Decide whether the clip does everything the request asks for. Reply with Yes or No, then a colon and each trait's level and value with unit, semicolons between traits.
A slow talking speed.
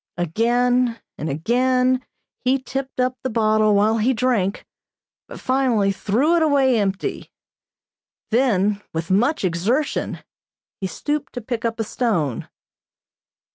Yes: slow, 125 wpm